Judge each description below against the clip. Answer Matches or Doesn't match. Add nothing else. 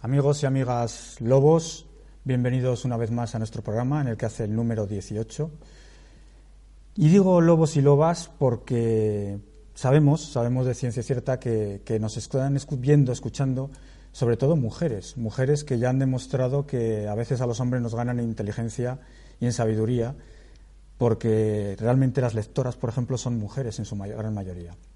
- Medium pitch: Doesn't match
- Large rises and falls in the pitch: Doesn't match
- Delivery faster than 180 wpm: Doesn't match